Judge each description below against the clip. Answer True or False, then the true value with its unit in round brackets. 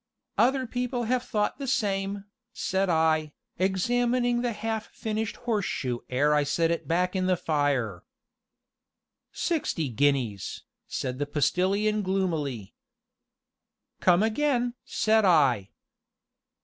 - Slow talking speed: True (110 wpm)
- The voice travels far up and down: True (7.2 semitones)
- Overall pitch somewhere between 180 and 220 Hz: True (190 Hz)